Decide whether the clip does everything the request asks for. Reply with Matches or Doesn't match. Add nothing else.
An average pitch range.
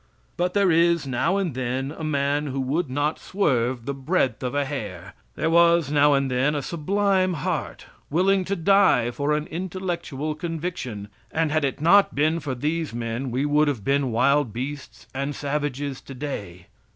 Matches